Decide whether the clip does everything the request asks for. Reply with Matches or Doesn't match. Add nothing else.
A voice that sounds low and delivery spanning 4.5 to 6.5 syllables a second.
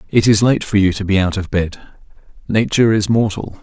Matches